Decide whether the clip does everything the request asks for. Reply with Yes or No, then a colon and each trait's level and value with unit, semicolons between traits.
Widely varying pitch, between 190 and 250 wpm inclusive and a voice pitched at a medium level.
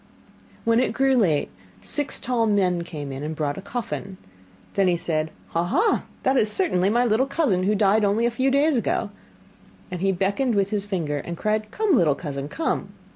No: wide, 5.9 semitones; average, 195 wpm; high, 205 Hz